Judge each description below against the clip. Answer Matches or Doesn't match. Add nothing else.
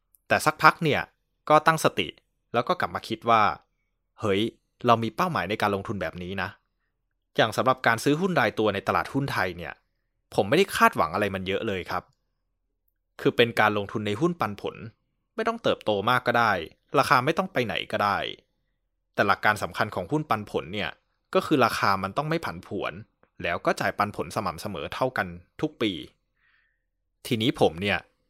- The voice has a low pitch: Matches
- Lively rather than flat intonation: Matches